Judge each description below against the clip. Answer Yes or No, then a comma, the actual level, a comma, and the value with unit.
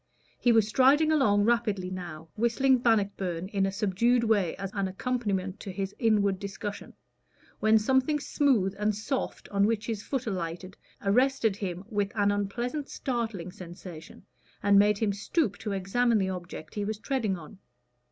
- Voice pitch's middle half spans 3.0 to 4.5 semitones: Yes, average, 3.6 semitones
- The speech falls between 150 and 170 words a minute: Yes, average, 160 wpm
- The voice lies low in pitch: No, high, 205 Hz